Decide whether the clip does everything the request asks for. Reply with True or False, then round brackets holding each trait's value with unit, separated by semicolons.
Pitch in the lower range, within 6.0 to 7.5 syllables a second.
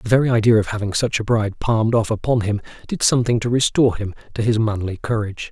True (110 Hz; 6.8 syllables/s)